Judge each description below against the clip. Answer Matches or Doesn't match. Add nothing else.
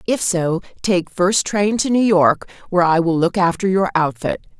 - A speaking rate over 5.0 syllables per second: Doesn't match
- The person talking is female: Matches